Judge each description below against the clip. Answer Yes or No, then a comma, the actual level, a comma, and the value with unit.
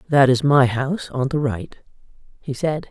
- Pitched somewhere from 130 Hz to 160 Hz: Yes, medium, 140 Hz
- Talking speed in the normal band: Yes, average, 185 wpm